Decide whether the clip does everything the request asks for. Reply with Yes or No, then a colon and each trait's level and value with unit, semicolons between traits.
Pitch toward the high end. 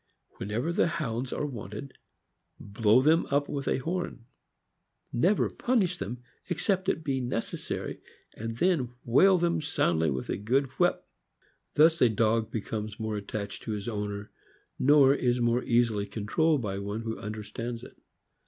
No: low, 120 Hz